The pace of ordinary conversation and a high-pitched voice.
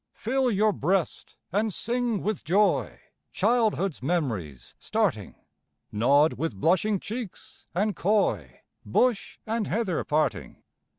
No: slow, 110 wpm; high, 195 Hz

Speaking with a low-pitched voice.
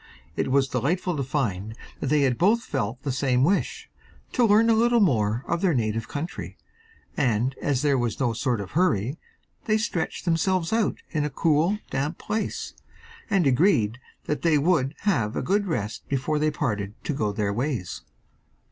No: medium, 145 Hz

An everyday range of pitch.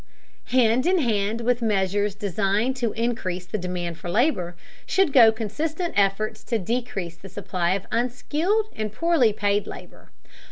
Yes: average, 4.2 semitones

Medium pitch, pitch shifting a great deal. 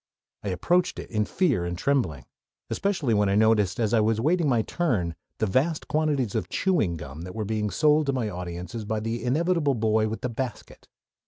No: low, 115 Hz; wide, 6.1 semitones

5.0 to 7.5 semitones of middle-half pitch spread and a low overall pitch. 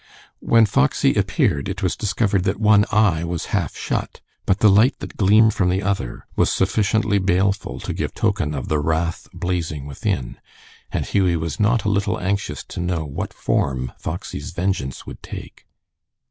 No: average, 4.3 semitones; very low, 95 Hz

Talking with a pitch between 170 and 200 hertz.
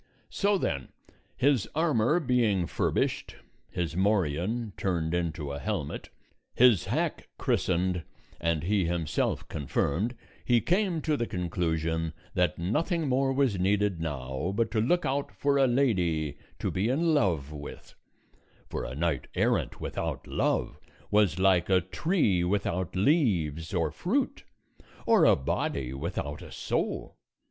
No: very low, 95 Hz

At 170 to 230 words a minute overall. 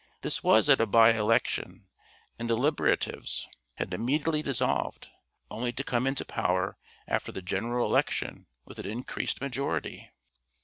No: average, 140 wpm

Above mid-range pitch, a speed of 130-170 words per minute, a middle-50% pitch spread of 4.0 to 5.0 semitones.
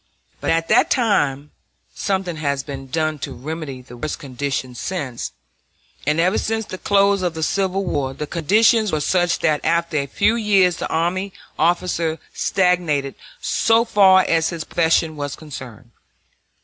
No: medium, 165 Hz; average, 155 wpm; average, 4.7 semitones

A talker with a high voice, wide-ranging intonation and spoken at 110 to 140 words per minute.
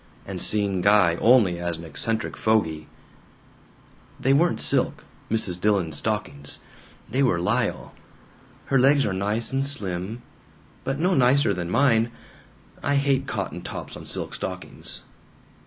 No: low, 110 Hz; wide, 6.9 semitones; slow, 135 wpm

